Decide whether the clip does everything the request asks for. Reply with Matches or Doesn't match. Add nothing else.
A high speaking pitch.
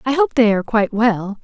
Matches